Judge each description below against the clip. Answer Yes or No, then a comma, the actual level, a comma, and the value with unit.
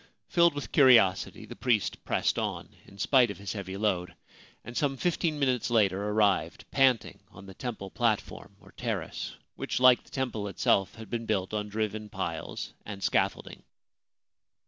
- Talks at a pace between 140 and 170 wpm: Yes, average, 160 wpm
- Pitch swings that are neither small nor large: Yes, average, 4.3 semitones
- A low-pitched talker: Yes, low, 110 Hz